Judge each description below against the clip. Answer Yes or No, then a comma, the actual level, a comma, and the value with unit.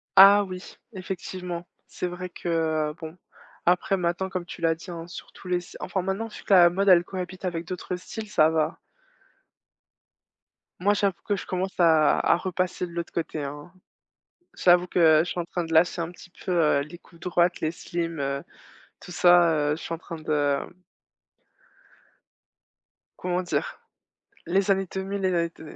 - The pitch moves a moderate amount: No, narrow, 2.0 semitones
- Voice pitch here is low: No, medium, 175 Hz